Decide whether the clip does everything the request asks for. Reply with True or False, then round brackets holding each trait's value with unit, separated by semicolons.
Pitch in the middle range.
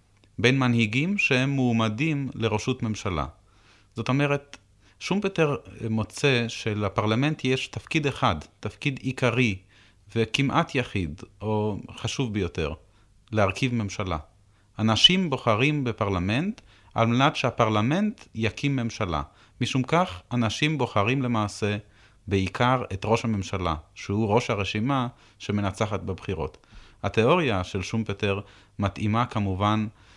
False (110 Hz)